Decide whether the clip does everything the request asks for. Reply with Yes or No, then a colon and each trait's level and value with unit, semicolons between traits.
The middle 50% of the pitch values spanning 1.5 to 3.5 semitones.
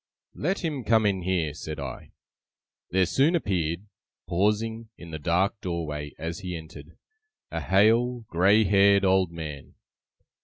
No: average, 4.5 semitones